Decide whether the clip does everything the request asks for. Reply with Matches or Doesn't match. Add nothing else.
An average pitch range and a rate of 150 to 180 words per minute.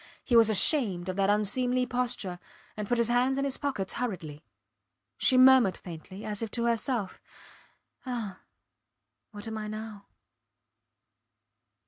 Doesn't match